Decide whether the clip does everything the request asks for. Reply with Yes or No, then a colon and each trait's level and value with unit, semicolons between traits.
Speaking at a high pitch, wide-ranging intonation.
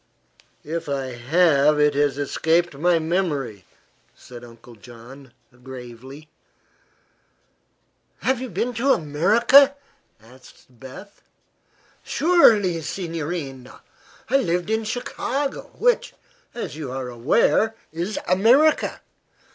No: medium, 160 Hz; wide, 8.3 semitones